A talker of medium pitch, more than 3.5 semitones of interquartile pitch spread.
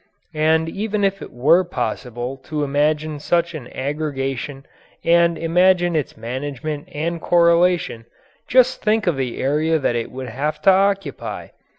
Yes: medium, 155 Hz; average, 4.3 semitones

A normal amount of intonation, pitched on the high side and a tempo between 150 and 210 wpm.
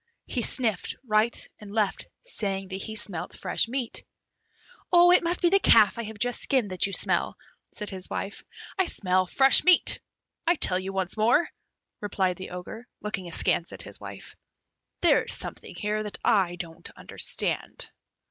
Yes: average, 4.4 semitones; high, 210 Hz; average, 165 wpm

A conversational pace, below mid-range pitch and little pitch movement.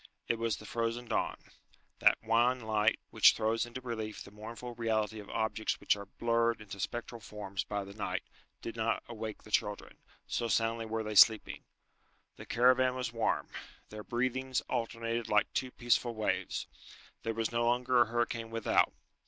Yes: average, 170 wpm; low, 115 Hz; narrow, 1.6 semitones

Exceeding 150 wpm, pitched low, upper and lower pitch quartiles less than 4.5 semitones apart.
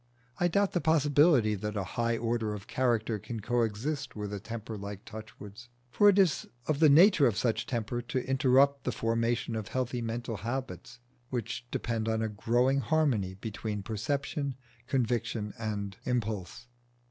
Yes: average, 160 wpm; low, 115 Hz; average, 3.7 semitones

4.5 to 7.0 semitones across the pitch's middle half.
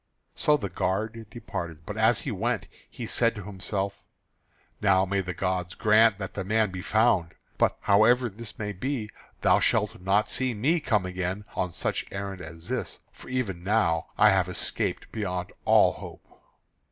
No: average, 3.4 semitones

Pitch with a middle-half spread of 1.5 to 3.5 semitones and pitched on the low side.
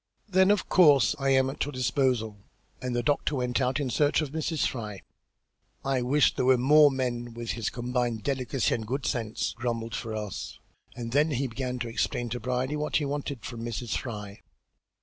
Yes: average, 2.9 semitones; low, 125 Hz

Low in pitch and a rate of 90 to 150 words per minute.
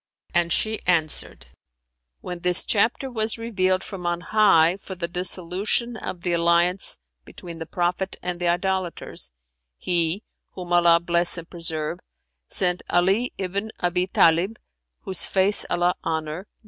No: medium, 180 Hz; slow, 135 wpm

